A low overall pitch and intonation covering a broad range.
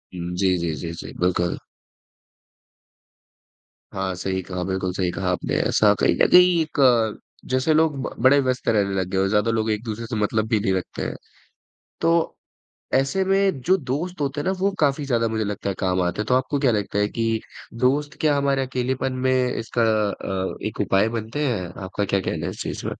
Yes: low, 115 Hz; wide, 6.2 semitones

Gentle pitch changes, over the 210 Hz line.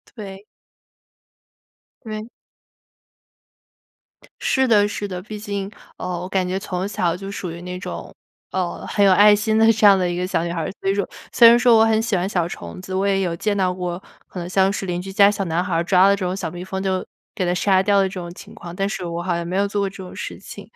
No: narrow, 2.1 semitones; high, 190 Hz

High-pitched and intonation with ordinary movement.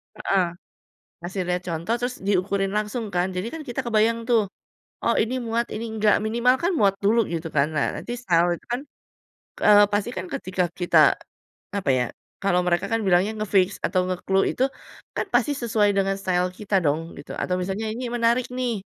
Yes: high, 200 Hz; average, 4.0 semitones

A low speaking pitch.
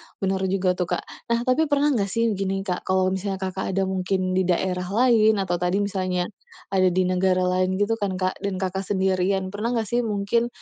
No: high, 190 Hz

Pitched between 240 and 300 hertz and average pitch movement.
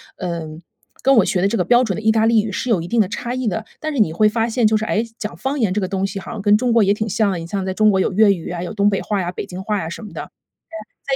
No: high, 210 Hz; average, 3.0 semitones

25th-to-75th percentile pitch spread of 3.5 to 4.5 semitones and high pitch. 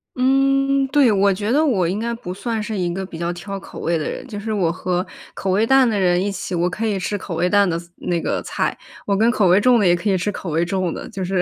Yes: average, 4.0 semitones; high, 195 Hz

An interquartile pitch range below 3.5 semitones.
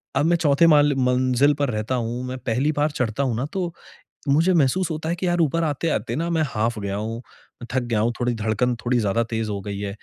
No: average, 5.1 semitones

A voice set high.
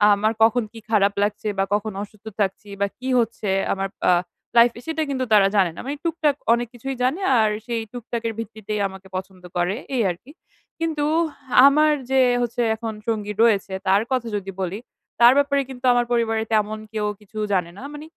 Yes: high, 225 Hz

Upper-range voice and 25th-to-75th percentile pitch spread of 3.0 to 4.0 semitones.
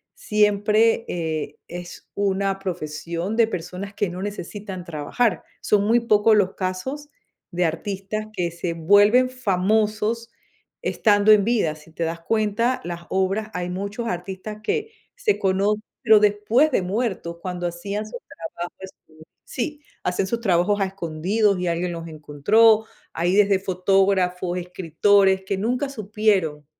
Yes: high, 195 Hz; average, 3.4 semitones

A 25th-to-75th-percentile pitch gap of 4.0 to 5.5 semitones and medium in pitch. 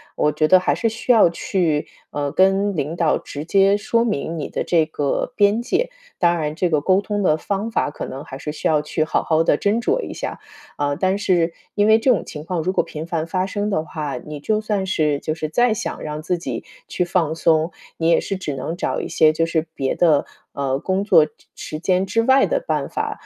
Yes: average, 4.6 semitones; medium, 170 Hz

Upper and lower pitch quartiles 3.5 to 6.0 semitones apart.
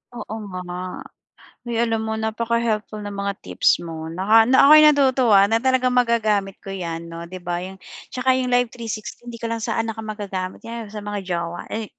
Yes: average, 3.9 semitones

